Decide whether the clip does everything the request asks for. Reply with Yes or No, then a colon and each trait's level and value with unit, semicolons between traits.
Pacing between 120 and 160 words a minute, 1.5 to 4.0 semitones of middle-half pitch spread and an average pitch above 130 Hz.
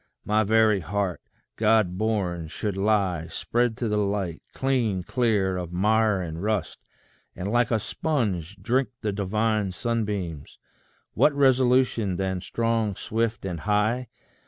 No: slow, 135 wpm; average, 3.3 semitones; low, 105 Hz